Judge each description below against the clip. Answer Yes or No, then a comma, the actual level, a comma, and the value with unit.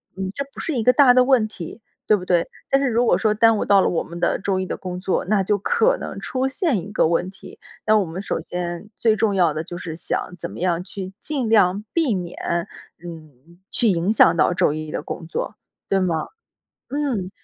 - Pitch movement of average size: Yes, average, 4.6 semitones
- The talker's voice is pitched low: No, high, 195 Hz